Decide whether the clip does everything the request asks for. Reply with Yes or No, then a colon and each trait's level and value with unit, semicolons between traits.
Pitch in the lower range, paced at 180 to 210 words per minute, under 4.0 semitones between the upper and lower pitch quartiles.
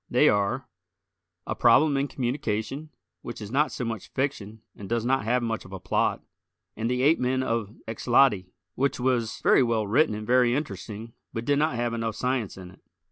Yes: low, 120 Hz; average, 190 wpm; average, 3.3 semitones